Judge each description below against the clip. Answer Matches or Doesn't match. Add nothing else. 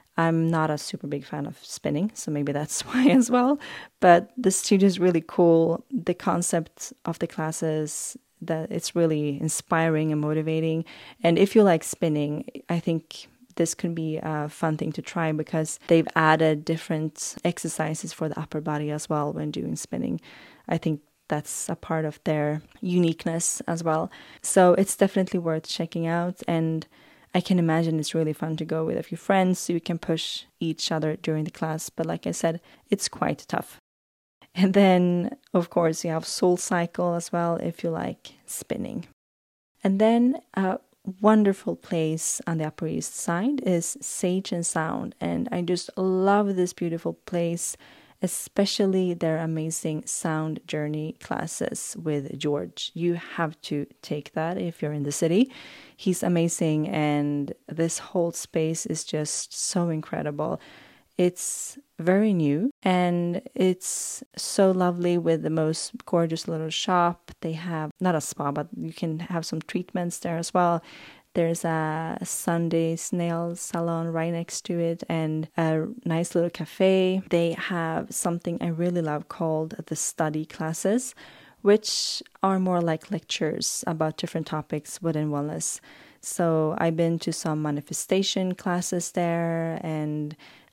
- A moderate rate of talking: Matches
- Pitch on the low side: Doesn't match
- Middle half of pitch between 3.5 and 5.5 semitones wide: Doesn't match